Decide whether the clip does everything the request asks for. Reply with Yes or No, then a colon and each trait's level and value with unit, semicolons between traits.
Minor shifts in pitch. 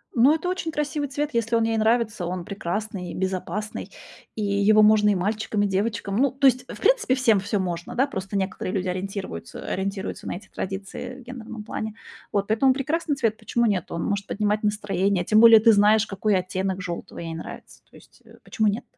No: average, 3.2 semitones